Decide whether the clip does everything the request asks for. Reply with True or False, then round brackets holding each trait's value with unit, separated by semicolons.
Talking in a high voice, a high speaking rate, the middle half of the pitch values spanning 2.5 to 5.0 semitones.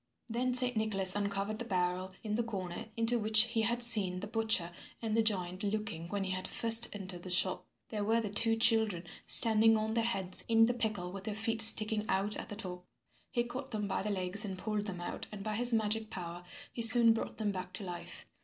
True (215 Hz; 225 wpm; 2.9 semitones)